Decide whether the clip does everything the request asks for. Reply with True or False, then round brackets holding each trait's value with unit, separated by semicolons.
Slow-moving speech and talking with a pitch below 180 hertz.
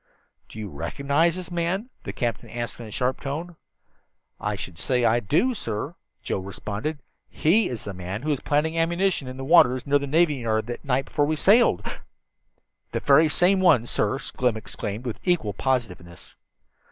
False (175 wpm; 135 Hz)